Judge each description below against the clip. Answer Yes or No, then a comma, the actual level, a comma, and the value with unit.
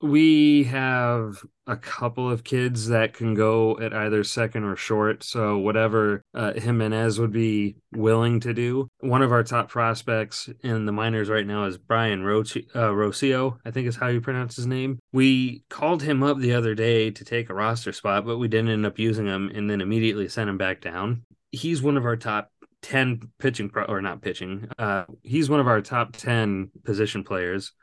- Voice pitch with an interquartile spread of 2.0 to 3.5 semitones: Yes, average, 2.8 semitones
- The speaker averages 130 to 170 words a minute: No, average, 200 wpm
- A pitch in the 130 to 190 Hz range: No, low, 115 Hz